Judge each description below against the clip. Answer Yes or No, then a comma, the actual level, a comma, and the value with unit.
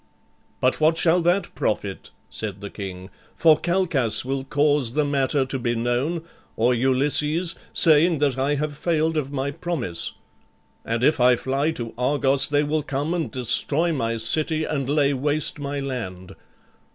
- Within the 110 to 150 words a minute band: No, average, 160 wpm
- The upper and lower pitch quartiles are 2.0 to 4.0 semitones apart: Yes, average, 3.7 semitones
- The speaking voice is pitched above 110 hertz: Yes, medium, 140 Hz